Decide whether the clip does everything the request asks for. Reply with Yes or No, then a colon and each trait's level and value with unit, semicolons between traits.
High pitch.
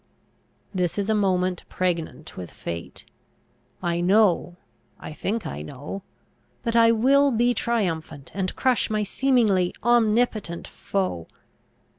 Yes: high, 195 Hz